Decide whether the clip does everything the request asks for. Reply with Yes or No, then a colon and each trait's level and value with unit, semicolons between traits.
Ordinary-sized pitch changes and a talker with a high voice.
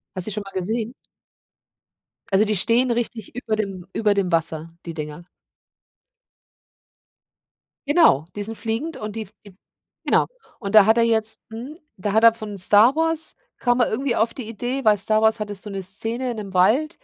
Yes: average, 3.1 semitones; high, 220 Hz